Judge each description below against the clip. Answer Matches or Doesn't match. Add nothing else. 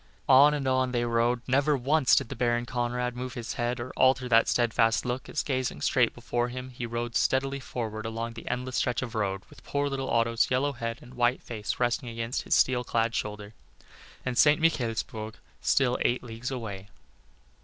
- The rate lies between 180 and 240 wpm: Matches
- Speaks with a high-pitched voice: Doesn't match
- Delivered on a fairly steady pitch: Matches